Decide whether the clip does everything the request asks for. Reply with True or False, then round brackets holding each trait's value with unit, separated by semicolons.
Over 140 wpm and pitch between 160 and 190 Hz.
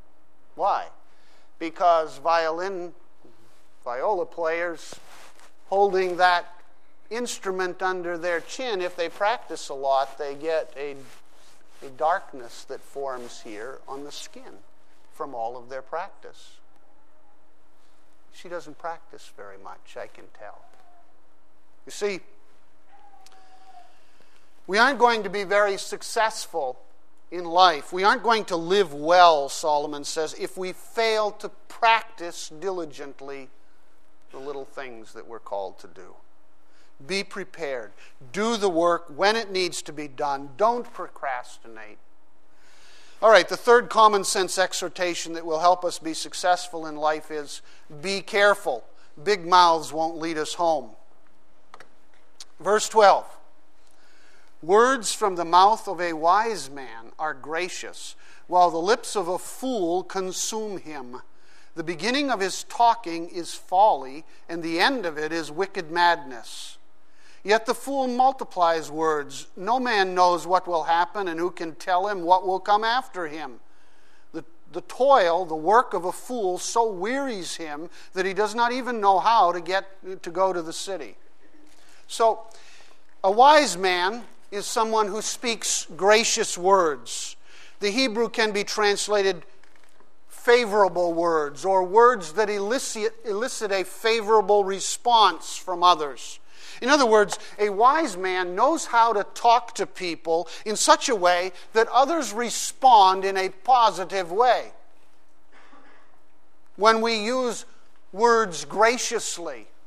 False (135 wpm; 185 Hz)